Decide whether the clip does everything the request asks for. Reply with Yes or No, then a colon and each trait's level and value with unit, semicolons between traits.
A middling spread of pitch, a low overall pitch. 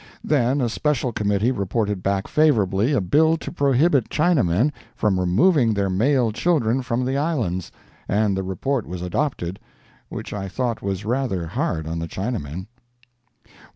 No: wide, 6.2 semitones; low, 110 Hz